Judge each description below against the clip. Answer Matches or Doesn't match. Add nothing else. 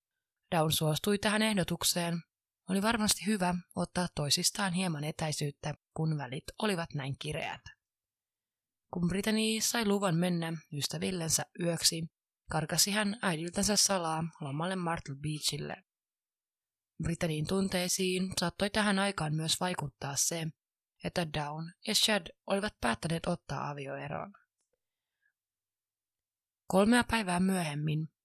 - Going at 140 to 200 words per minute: Doesn't match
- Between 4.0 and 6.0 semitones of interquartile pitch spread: Matches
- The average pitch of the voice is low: Doesn't match